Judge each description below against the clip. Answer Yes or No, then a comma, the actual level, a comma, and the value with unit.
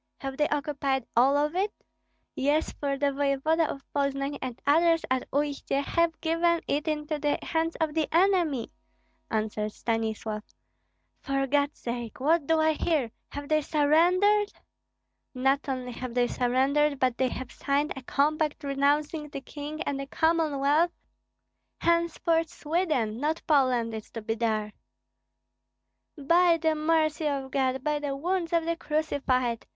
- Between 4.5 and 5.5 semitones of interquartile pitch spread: No, average, 3.2 semitones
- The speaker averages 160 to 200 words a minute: No, average, 145 wpm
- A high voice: Yes, very high, 290 Hz